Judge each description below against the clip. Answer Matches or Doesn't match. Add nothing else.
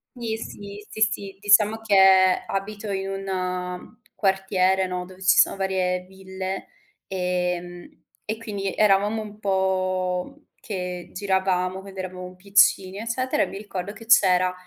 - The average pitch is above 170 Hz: Matches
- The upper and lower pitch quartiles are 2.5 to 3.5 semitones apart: Doesn't match